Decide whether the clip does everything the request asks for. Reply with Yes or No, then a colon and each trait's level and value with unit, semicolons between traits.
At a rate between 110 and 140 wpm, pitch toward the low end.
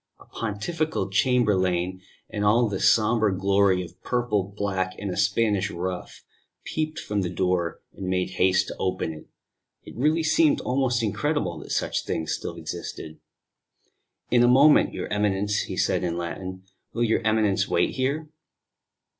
No: average, 155 wpm; low, 100 Hz